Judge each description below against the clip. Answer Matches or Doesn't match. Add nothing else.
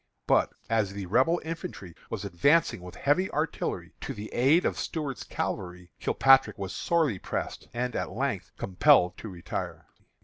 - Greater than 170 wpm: Doesn't match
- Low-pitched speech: Matches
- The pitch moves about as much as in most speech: Doesn't match